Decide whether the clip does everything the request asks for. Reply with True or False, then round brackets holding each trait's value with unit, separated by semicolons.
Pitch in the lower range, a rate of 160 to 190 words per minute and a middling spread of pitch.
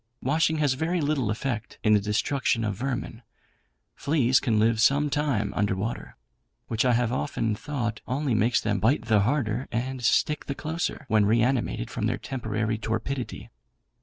True (120 Hz; 165 wpm; 4.2 semitones)